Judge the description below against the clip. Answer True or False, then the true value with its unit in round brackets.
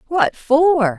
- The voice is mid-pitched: False (275 Hz)